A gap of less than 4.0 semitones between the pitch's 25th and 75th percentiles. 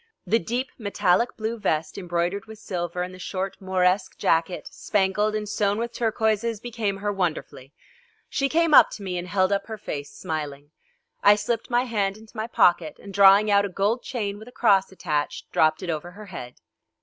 Yes: average, 3.4 semitones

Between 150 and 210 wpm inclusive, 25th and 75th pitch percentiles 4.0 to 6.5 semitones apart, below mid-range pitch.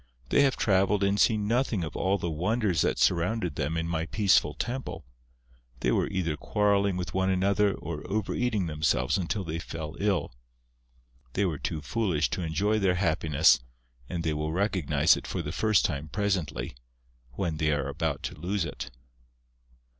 Yes: average, 170 wpm; average, 4.3 semitones; very low, 90 Hz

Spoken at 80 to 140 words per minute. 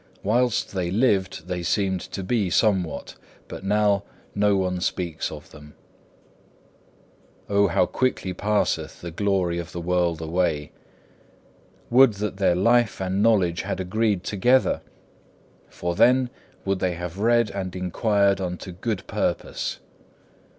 Yes: slow, 135 wpm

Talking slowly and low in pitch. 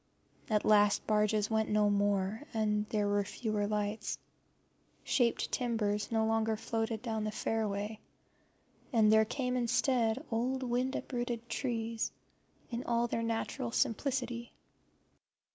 No: slow, 125 wpm; high, 225 Hz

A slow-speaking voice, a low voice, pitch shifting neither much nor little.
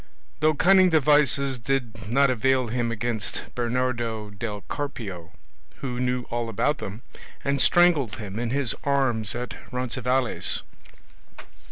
Yes: slow, 125 wpm; low, 125 Hz; average, 3.4 semitones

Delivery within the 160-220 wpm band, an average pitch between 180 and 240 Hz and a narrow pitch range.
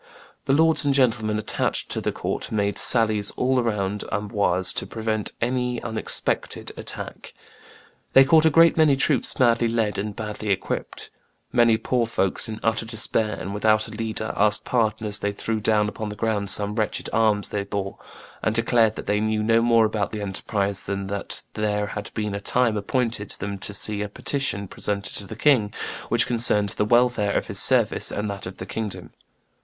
No: average, 185 wpm; low, 110 Hz; narrow, 2.1 semitones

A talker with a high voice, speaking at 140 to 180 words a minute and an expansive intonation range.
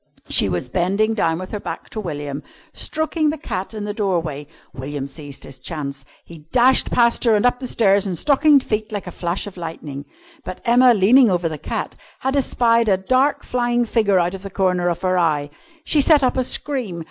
No: high, 195 Hz; fast, 205 wpm; wide, 6.4 semitones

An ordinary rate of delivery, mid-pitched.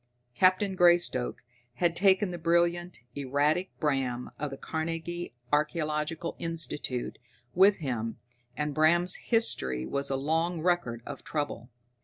No: slow, 120 wpm; medium, 160 Hz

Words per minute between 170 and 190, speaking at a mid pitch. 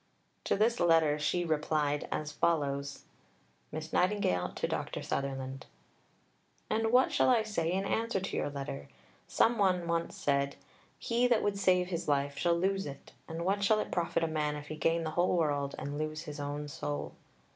Yes: average, 180 wpm; medium, 160 Hz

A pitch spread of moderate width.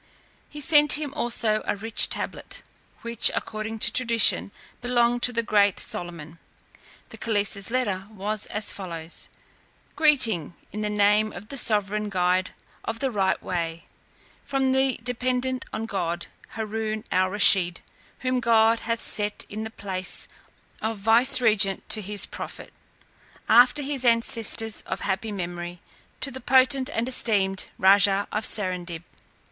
Yes: average, 3.8 semitones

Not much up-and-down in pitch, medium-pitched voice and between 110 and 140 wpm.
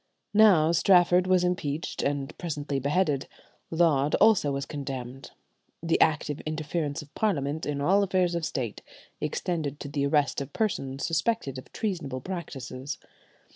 No: average, 4.1 semitones; medium, 150 Hz; slow, 135 wpm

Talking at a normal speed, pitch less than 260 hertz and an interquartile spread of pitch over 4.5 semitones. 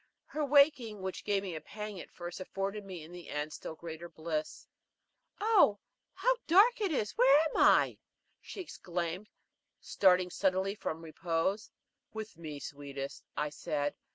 Yes: average, 155 wpm; medium, 185 Hz; average, 4.9 semitones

